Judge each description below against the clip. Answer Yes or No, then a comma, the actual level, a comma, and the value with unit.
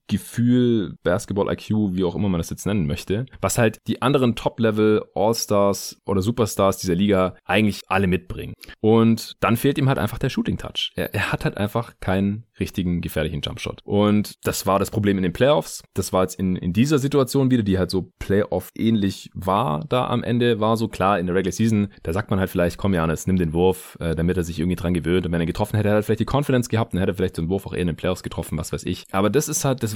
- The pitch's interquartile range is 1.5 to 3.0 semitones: No, average, 3.7 semitones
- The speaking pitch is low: Yes, low, 100 Hz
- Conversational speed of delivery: No, fast, 245 wpm